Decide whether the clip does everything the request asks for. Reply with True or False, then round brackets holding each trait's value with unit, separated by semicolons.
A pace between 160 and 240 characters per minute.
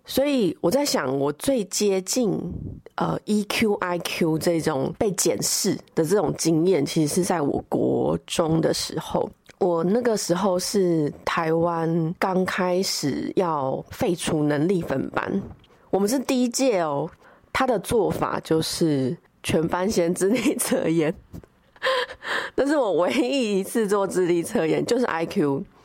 True (205 characters per minute)